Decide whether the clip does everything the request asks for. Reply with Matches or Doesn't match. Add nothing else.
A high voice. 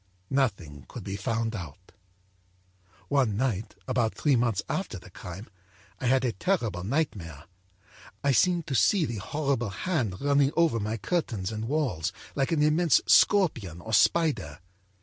Doesn't match